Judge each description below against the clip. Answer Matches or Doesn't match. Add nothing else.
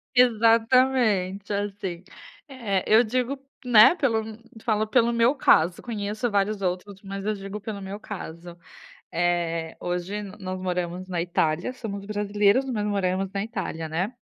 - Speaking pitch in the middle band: Doesn't match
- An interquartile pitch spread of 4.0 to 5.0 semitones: Doesn't match